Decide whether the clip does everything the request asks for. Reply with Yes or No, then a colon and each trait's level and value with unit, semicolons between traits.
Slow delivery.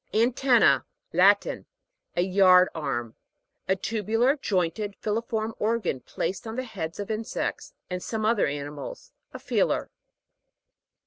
Yes: slow, 120 wpm